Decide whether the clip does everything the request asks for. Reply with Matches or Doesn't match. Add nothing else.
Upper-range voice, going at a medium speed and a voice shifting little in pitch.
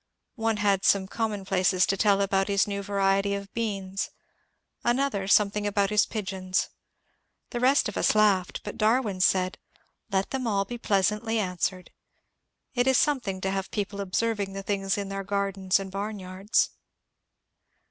Matches